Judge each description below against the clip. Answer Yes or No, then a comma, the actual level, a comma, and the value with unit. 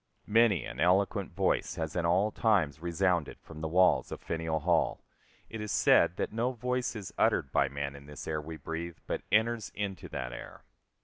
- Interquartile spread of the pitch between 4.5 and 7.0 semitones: Yes, average, 4.8 semitones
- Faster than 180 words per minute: Yes, average, 190 wpm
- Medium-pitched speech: No, very low, 85 Hz